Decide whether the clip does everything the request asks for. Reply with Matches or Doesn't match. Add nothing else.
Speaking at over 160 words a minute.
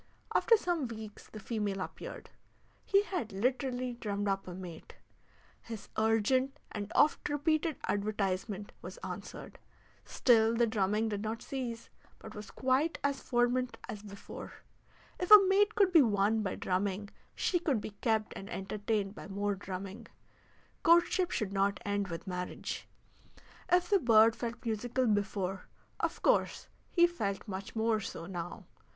Doesn't match